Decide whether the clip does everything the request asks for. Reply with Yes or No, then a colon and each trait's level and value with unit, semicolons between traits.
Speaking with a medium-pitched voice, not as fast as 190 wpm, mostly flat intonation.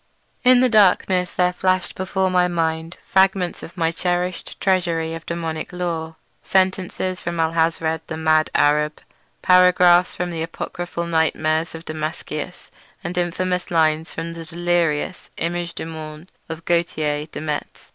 Yes: medium, 170 Hz; average, 140 wpm; narrow, 1.9 semitones